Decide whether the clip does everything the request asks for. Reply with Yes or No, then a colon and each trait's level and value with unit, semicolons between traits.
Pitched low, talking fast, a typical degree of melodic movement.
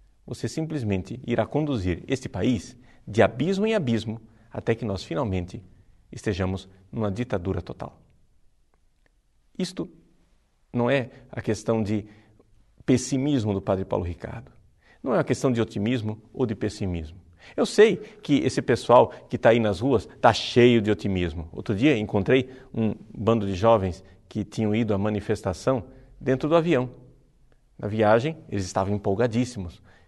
No: low, 110 Hz; average, 145 wpm; average, 4.6 semitones